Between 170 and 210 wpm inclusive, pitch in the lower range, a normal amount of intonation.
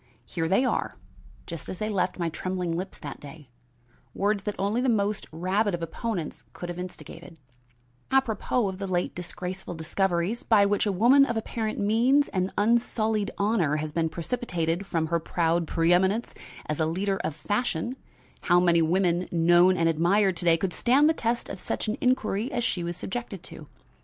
No: average, 180 wpm; high, 190 Hz; average, 4.2 semitones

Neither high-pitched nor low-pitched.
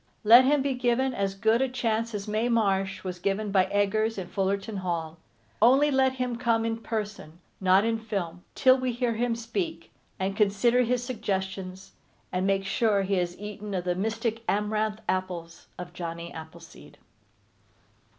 No: high, 210 Hz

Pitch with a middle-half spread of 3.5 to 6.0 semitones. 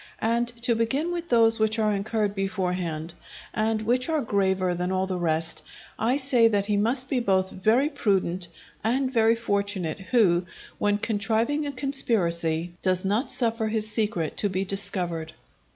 Yes: average, 3.9 semitones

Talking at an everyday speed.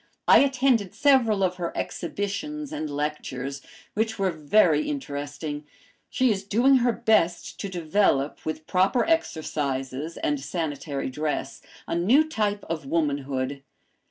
No: slow, 130 wpm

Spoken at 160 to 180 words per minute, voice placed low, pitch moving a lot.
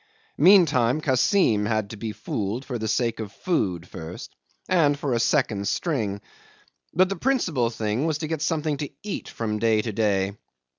Yes: average, 170 wpm; low, 120 Hz; wide, 6.5 semitones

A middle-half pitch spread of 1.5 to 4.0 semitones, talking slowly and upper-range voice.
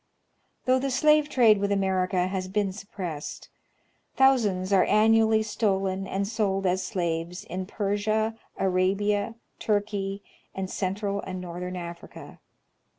Yes: narrow, 2.6 semitones; slow, 120 wpm; high, 195 Hz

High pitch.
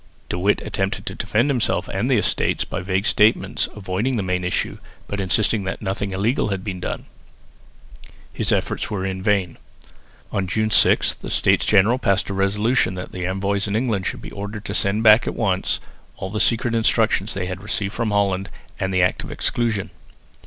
No: low, 100 Hz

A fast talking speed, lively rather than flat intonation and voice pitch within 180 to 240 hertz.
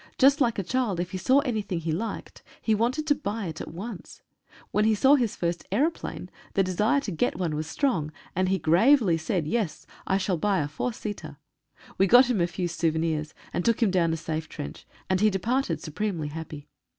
Yes: fast, 210 wpm; wide, 5.9 semitones; high, 190 Hz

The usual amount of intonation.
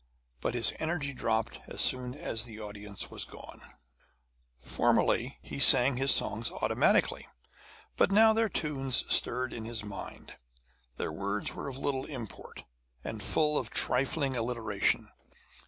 Yes: average, 4.1 semitones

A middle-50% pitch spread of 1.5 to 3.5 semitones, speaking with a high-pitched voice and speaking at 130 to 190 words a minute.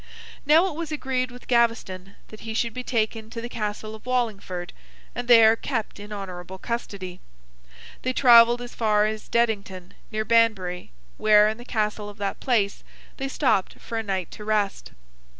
Yes: average, 2.9 semitones; high, 220 Hz; average, 170 wpm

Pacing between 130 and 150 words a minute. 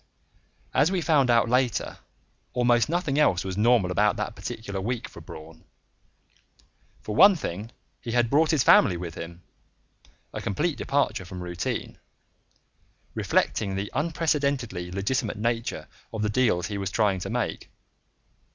Yes: average, 145 wpm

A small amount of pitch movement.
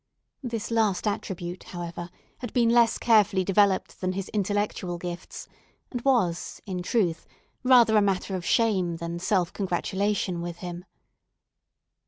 No: average, 3.8 semitones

